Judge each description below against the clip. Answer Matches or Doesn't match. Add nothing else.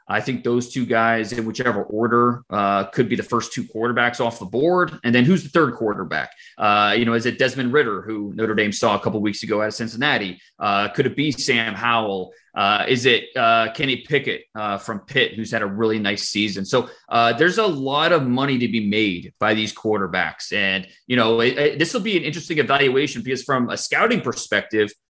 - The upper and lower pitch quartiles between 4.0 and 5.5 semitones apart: Doesn't match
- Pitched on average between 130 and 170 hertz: Doesn't match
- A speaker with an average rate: Doesn't match